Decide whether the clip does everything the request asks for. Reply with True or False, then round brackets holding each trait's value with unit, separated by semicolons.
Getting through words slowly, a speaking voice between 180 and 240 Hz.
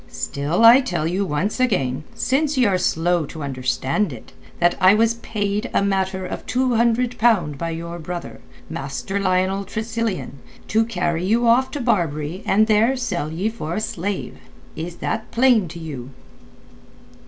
False (165 wpm; 190 Hz)